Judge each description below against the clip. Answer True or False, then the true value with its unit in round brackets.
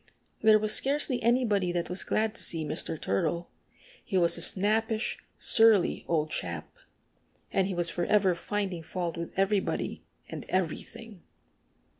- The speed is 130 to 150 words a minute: True (140 wpm)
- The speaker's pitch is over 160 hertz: True (190 Hz)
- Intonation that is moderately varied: True (4.2 semitones)